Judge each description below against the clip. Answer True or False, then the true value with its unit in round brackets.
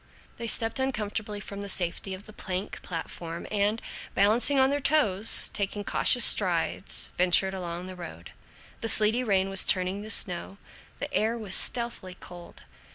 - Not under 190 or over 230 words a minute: False (160 wpm)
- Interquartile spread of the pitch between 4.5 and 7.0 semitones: False (3.3 semitones)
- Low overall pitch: False (200 Hz)